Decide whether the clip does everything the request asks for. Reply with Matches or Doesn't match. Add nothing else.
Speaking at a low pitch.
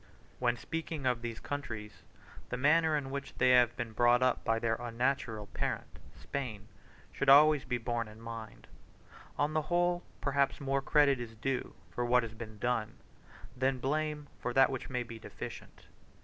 Matches